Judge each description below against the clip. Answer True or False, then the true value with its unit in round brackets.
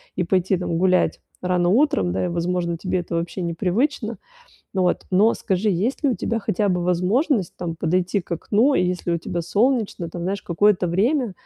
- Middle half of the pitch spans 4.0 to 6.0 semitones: False (3.3 semitones)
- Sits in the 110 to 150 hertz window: False (185 Hz)